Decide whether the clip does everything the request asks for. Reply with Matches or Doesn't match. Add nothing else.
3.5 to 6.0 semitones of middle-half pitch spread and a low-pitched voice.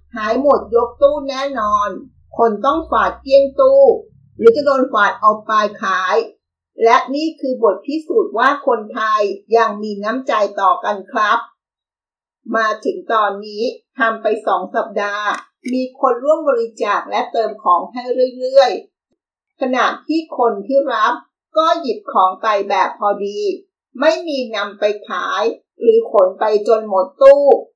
Doesn't match